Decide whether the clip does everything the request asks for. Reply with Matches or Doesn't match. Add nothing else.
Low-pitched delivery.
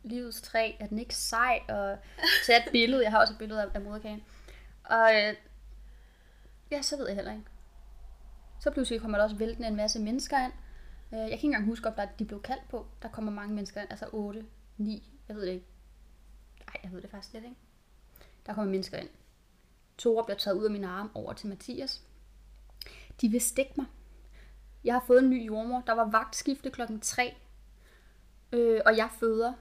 Doesn't match